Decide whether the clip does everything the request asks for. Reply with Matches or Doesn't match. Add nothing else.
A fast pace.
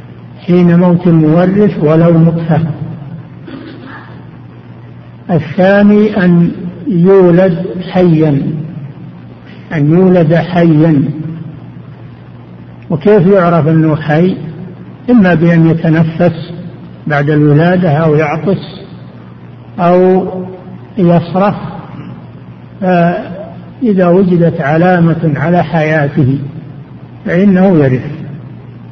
Doesn't match